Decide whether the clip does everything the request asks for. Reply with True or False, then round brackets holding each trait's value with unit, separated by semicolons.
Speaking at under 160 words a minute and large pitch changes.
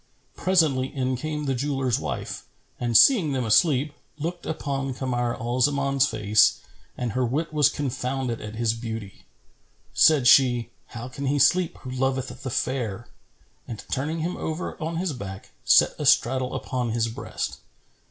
False (150 wpm; 3.4 semitones)